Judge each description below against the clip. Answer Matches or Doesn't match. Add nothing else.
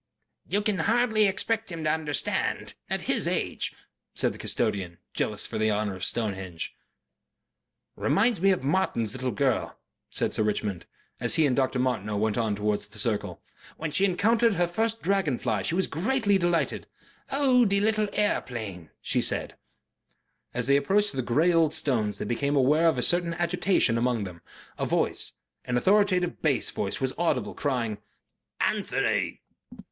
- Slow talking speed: Doesn't match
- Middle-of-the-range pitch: Matches